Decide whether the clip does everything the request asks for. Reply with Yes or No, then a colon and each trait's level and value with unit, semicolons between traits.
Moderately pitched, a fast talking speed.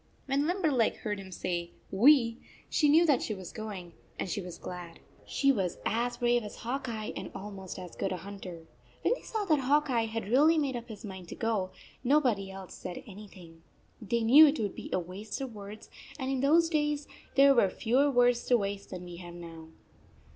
No: high, 225 Hz; fast, 210 wpm